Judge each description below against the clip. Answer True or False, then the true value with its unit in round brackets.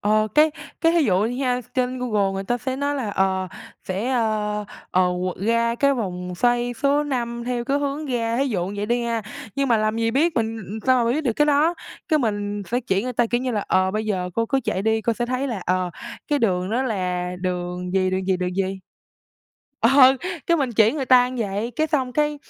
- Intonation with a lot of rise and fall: False (4.8 semitones)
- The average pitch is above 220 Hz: True (230 Hz)